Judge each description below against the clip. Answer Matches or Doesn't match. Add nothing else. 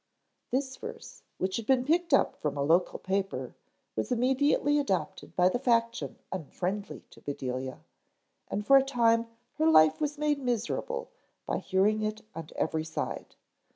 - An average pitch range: Doesn't match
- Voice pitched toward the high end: Matches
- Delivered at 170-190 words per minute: Doesn't match